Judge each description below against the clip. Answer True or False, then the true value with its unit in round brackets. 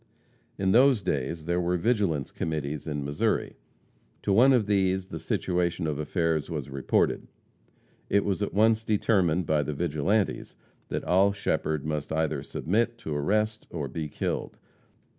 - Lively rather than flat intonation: False (5.0 semitones)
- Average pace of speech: True (150 wpm)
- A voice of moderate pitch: False (85 Hz)